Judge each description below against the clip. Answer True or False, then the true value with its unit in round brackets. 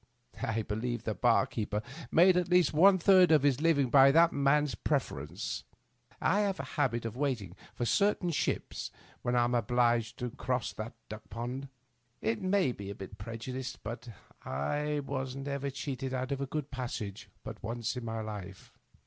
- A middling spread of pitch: True (4.2 semitones)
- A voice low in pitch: True (130 Hz)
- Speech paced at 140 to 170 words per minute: False (180 wpm)